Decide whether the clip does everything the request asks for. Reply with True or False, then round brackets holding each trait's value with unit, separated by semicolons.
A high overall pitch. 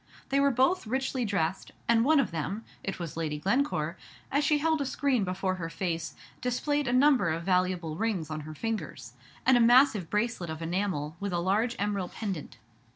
True (200 Hz)